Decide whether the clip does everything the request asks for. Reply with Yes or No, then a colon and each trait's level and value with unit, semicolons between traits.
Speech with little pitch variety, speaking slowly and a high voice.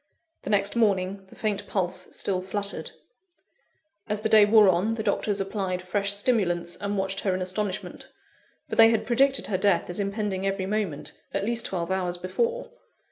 No: narrow, 2.3 semitones; average, 175 wpm; high, 200 Hz